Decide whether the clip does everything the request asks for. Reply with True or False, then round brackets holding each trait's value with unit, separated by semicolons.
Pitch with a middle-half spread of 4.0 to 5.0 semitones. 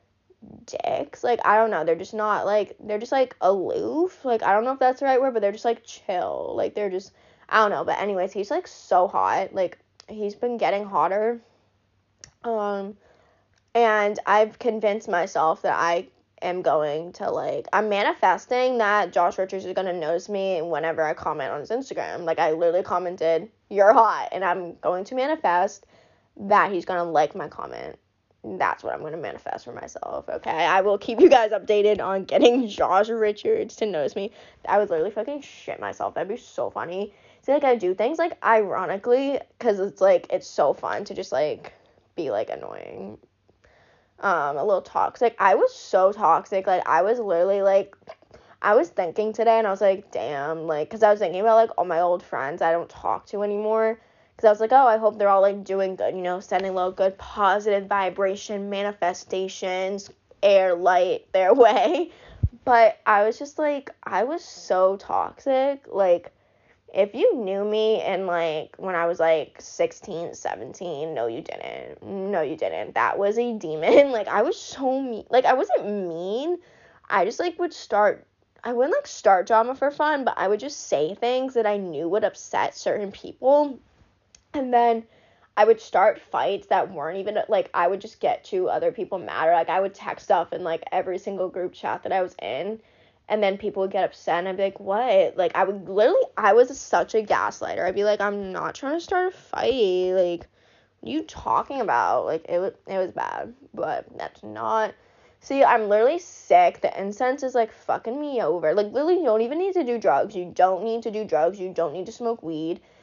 True (4.6 semitones)